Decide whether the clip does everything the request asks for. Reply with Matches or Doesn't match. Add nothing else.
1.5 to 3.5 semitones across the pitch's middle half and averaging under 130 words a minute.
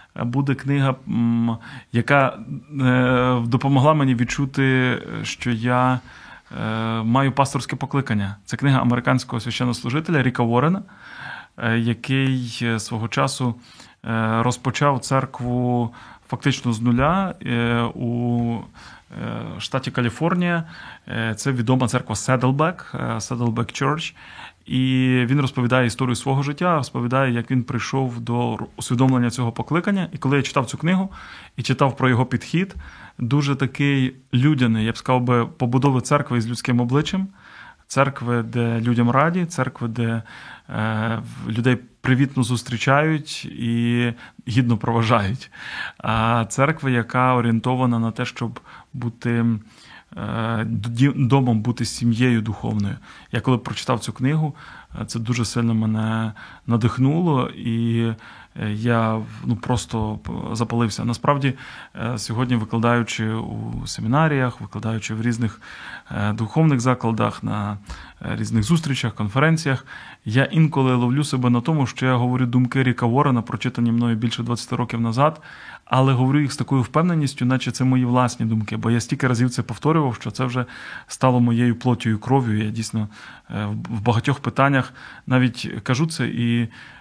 Matches